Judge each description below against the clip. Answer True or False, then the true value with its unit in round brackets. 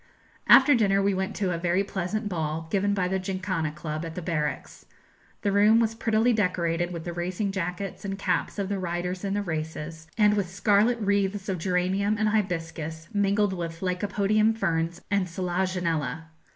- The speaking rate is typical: True (175 wpm)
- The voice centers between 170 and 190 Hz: True (185 Hz)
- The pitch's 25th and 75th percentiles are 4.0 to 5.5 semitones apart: False (3.2 semitones)